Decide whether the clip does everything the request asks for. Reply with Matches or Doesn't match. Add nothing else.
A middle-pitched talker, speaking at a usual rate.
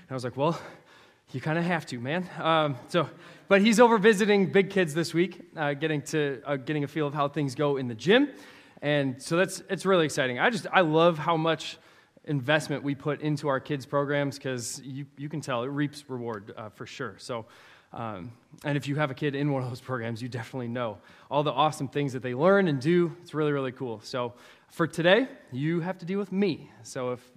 Doesn't match